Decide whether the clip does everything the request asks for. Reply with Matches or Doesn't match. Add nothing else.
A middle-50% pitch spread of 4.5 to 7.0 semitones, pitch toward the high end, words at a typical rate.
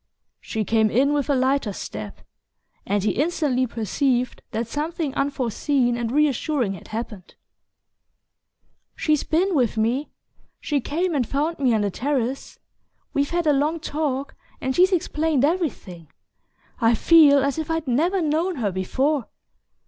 Matches